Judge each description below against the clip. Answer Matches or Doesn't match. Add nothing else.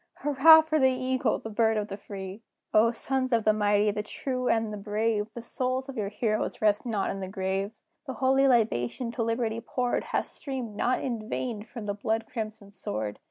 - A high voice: Matches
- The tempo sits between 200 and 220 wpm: Matches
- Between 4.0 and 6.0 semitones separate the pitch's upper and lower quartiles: Doesn't match